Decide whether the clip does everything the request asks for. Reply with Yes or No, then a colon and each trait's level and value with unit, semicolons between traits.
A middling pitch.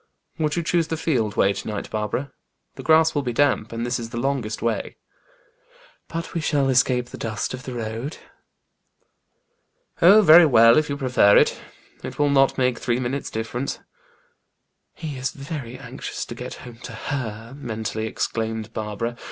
No: low, 125 Hz